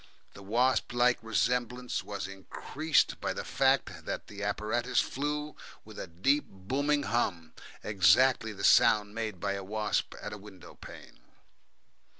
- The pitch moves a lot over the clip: No, average, 4.2 semitones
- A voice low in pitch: Yes, low, 110 Hz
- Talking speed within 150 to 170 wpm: No, average, 140 wpm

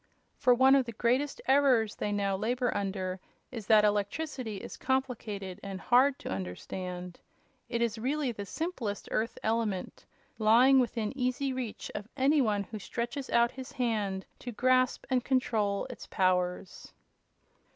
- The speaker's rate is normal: Yes, average, 150 wpm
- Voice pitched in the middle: No, high, 230 Hz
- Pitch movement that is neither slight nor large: Yes, average, 4.2 semitones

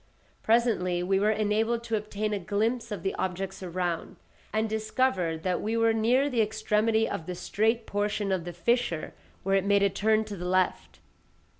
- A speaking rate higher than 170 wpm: Yes, average, 180 wpm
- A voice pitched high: Yes, high, 210 Hz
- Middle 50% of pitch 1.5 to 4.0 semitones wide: Yes, average, 3.1 semitones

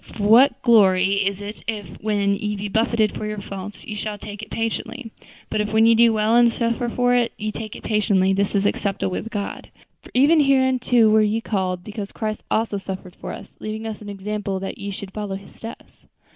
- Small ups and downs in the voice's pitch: Yes, narrow, 2.2 semitones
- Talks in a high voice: Yes, high, 210 Hz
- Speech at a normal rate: No, fast, 215 wpm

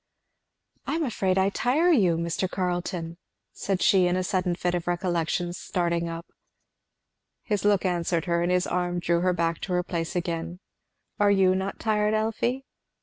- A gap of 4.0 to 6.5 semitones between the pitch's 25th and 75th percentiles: No, narrow, 2.4 semitones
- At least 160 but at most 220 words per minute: Yes, average, 170 wpm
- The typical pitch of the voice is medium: Yes, medium, 180 Hz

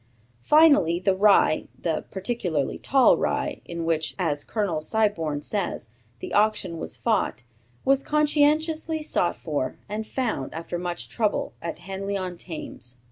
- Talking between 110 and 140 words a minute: Yes, slow, 135 wpm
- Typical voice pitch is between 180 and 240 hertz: Yes, high, 190 Hz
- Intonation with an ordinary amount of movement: No, wide, 5.9 semitones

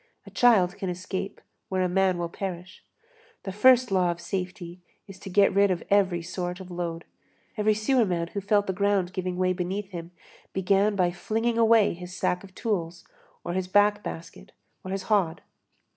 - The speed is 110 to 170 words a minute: No, average, 180 wpm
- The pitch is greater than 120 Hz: Yes, high, 190 Hz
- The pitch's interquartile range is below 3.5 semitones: Yes, narrow, 2.4 semitones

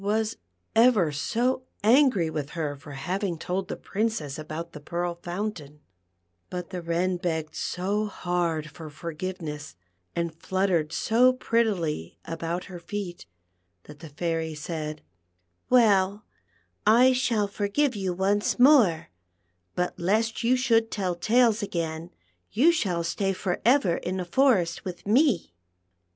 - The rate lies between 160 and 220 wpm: No, average, 140 wpm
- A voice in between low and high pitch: Yes, medium, 180 Hz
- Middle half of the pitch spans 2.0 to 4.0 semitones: No, average, 4.9 semitones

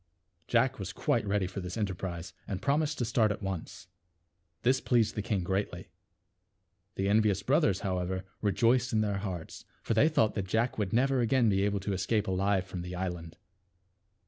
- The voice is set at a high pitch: No, low, 100 Hz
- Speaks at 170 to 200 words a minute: Yes, average, 180 wpm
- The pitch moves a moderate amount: Yes, average, 3.5 semitones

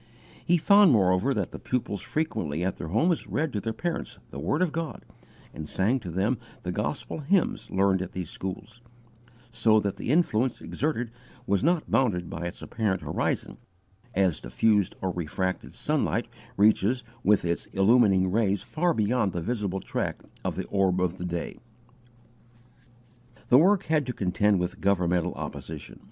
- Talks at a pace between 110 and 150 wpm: No, average, 160 wpm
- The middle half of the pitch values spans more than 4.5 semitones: Yes, wide, 5.6 semitones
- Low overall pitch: Yes, low, 100 Hz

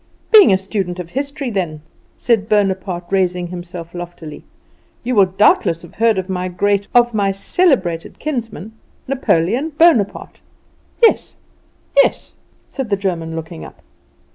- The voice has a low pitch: No, high, 195 Hz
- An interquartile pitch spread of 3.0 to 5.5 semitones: Yes, average, 5.1 semitones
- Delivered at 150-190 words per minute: No, slow, 135 wpm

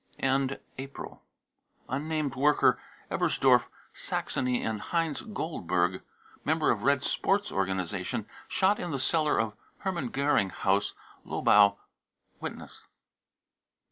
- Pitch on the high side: No, low, 135 Hz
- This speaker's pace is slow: Yes, slow, 105 wpm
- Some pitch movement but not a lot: No, wide, 7.3 semitones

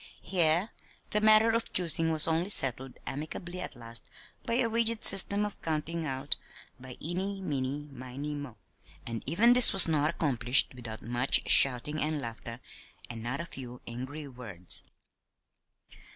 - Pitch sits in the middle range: Yes, medium, 150 Hz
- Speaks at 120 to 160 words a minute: Yes, average, 150 wpm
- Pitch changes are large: Yes, wide, 6.2 semitones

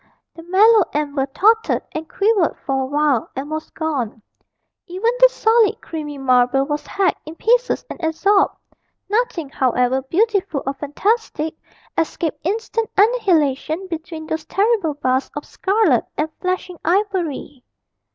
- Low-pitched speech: No, very high, 320 Hz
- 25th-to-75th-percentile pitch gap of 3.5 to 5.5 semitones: No, wide, 5.9 semitones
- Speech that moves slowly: Yes, slow, 130 wpm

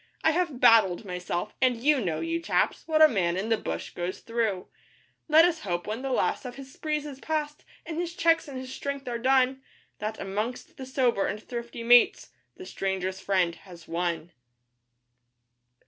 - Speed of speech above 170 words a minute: Yes, average, 180 wpm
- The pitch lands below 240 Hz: No, high, 245 Hz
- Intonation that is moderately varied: No, wide, 7.2 semitones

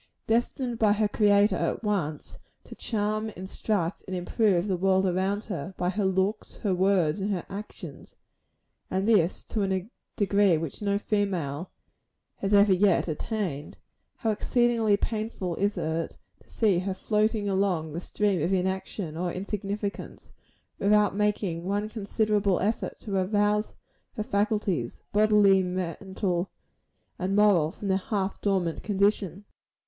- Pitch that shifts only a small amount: Yes, narrow, 2.3 semitones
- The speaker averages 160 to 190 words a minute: No, average, 140 wpm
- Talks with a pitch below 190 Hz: No, high, 200 Hz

